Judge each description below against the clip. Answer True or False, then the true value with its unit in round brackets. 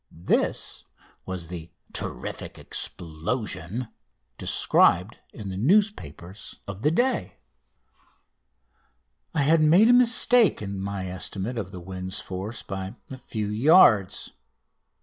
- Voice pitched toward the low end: True (100 Hz)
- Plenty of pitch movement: True (7.7 semitones)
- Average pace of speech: False (110 wpm)